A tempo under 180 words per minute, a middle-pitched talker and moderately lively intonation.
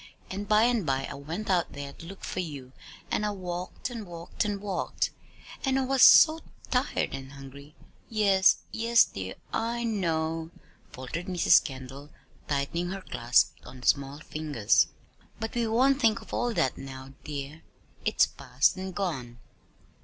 No: average, 165 wpm; medium, 175 Hz; wide, 7.5 semitones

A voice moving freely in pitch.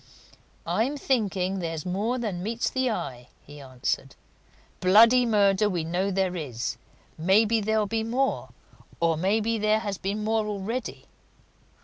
No: average, 3.7 semitones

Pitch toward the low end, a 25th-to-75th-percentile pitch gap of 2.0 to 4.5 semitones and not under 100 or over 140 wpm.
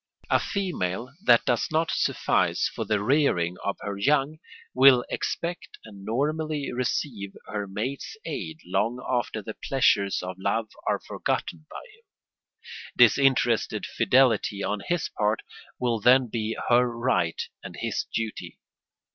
No: low, 120 Hz; average, 5.1 semitones; slow, 135 wpm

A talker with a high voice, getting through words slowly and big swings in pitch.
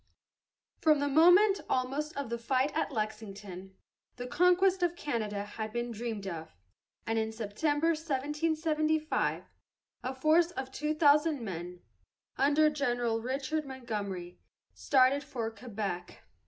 Yes: very high, 260 Hz; slow, 125 wpm; wide, 5.8 semitones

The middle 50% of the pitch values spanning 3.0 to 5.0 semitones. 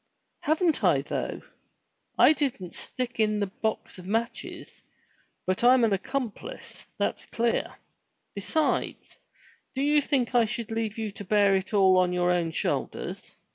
Yes: average, 4.7 semitones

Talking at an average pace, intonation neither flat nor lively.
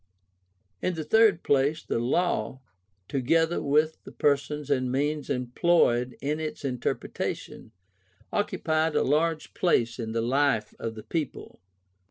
No: slow, 130 wpm; average, 4.1 semitones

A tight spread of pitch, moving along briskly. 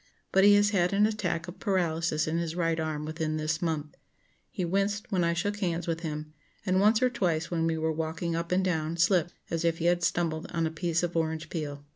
Yes: narrow, 2.3 semitones; fast, 230 wpm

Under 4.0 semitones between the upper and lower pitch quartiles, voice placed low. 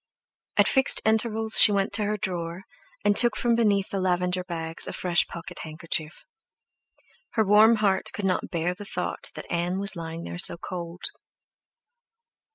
No: average, 3.6 semitones; high, 190 Hz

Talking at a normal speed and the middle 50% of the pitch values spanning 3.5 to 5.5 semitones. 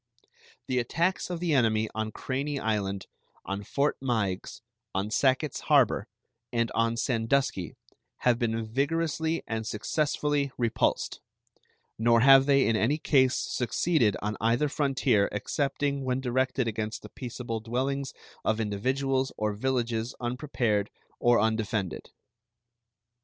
No: slow, 120 wpm; average, 3.8 semitones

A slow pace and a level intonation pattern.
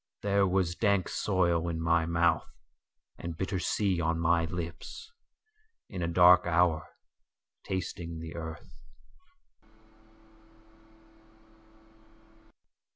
Yes: slow, 85 wpm; narrow, 2.3 semitones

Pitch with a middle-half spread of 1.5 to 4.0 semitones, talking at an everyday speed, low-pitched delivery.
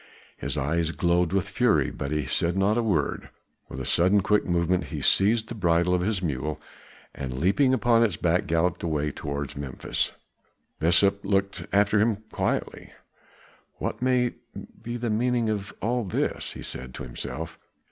No: average, 5.2 semitones; average, 165 wpm; very low, 90 Hz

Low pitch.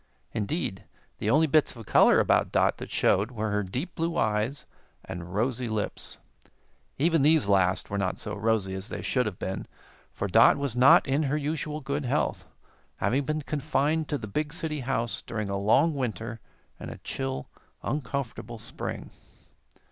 Yes: low, 120 Hz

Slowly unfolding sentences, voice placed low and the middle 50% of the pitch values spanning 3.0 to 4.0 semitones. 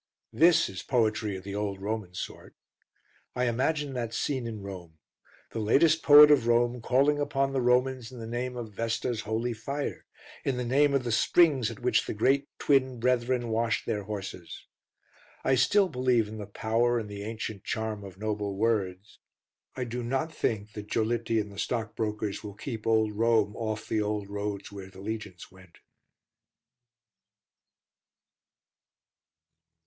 No: average, 160 wpm; low, 115 Hz; average, 3.3 semitones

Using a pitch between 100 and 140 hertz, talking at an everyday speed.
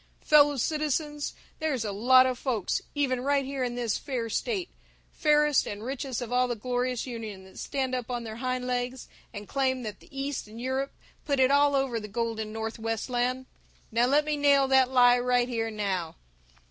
No: very high, 250 Hz; average, 190 wpm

